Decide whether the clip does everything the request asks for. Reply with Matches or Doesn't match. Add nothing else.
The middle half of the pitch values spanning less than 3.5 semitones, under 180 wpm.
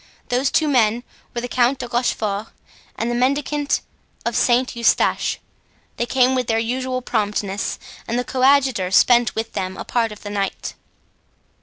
Matches